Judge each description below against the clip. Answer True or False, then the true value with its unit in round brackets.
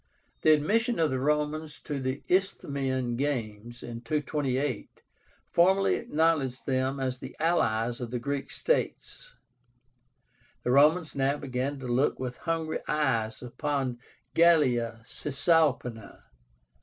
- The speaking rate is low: True (120 wpm)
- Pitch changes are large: False (3.9 semitones)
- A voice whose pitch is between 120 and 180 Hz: True (140 Hz)